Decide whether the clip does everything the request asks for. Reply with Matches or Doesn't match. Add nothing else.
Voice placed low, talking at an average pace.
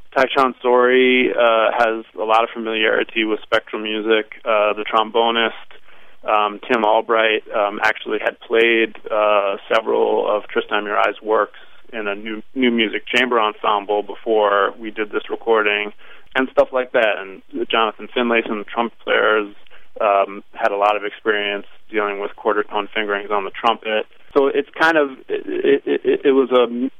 Matches